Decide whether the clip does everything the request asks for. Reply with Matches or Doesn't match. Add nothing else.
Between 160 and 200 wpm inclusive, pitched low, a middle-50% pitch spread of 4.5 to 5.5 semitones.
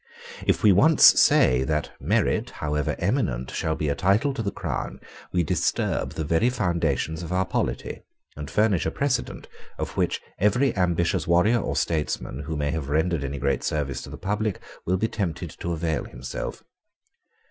Matches